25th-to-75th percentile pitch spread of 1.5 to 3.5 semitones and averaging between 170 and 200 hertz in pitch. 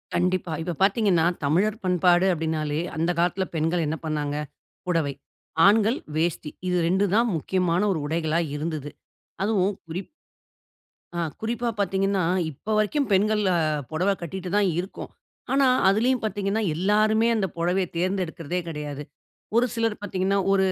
No: average, 3.9 semitones; medium, 185 Hz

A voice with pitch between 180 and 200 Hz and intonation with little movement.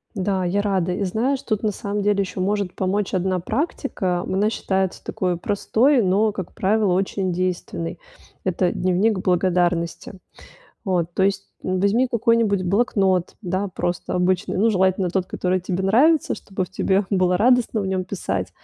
Yes: high, 190 Hz; narrow, 2.3 semitones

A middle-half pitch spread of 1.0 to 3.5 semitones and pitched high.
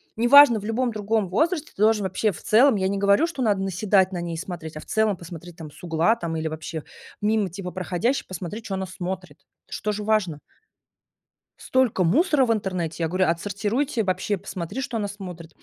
No: average, 4.0 semitones; high, 195 Hz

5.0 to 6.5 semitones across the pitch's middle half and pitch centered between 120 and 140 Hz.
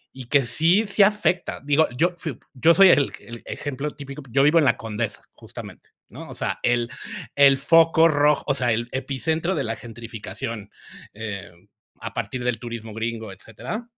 Yes: wide, 5.4 semitones; low, 135 Hz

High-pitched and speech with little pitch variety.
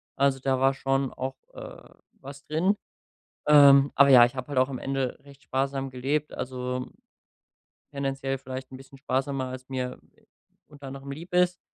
No: low, 135 Hz; narrow, 1.2 semitones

